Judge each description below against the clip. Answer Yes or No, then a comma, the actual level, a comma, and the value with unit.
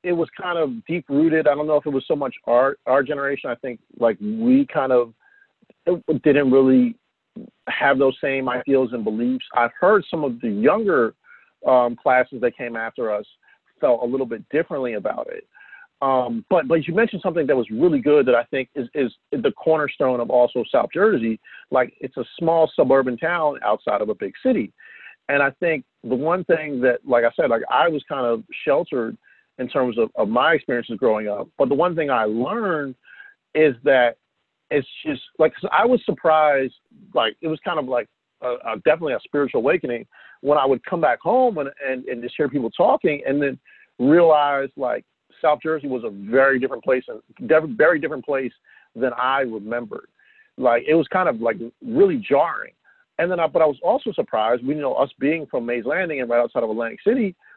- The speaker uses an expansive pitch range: Yes, wide, 6.7 semitones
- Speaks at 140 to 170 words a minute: No, average, 200 wpm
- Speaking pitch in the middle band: Yes, medium, 145 Hz